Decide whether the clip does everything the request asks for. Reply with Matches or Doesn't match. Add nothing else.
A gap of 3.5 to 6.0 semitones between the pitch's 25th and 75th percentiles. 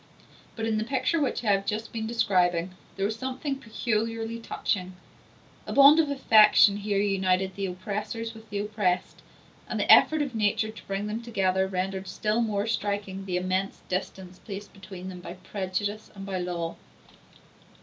Doesn't match